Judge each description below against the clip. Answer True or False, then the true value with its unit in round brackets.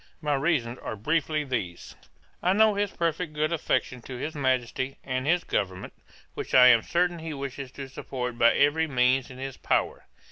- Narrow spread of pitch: False (4.1 semitones)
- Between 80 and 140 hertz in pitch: True (135 Hz)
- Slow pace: False (180 wpm)